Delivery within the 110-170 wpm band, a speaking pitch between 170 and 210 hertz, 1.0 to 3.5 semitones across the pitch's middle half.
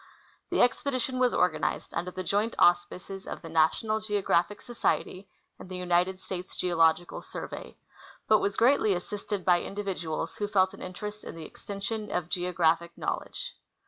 Yes: average, 155 wpm; medium, 185 Hz; average, 2.9 semitones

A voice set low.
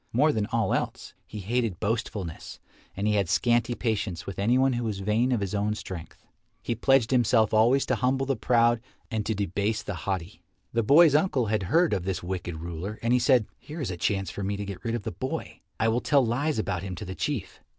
Yes: low, 110 Hz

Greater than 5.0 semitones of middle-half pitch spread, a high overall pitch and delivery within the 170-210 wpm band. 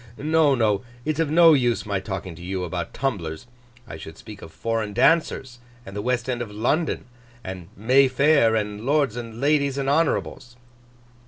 No: wide, 5.5 semitones; low, 120 Hz; average, 175 wpm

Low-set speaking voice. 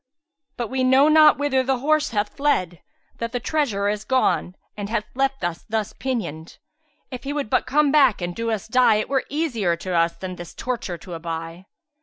No: high, 230 Hz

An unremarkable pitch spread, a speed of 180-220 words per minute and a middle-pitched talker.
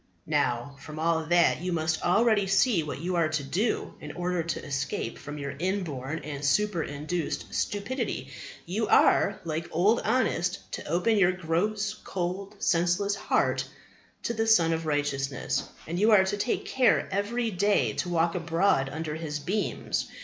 No: average, 4.6 semitones; average, 160 wpm; medium, 175 Hz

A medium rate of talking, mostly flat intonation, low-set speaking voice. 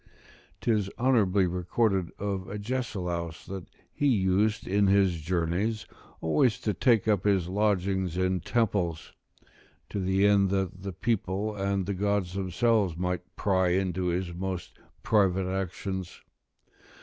No: slow, 125 wpm; narrow, 2.1 semitones; very low, 95 Hz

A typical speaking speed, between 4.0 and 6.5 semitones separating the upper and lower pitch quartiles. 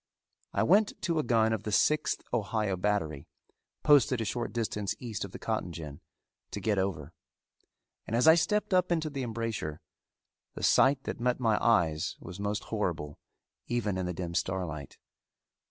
Yes: average, 170 wpm; average, 5.3 semitones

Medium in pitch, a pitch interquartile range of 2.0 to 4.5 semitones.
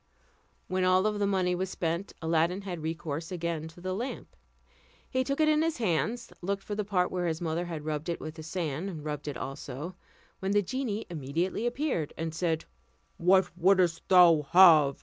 Yes: medium, 175 Hz; average, 3.4 semitones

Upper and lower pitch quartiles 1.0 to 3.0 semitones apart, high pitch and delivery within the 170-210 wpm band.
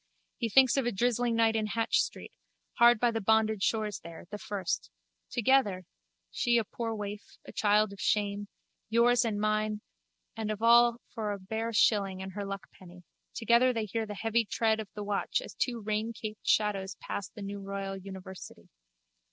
Yes: narrow, 2.4 semitones; high, 215 Hz; average, 180 wpm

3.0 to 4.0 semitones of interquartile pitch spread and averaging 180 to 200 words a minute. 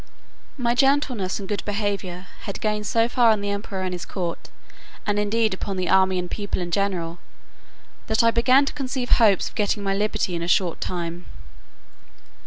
Yes: average, 3.6 semitones; average, 185 wpm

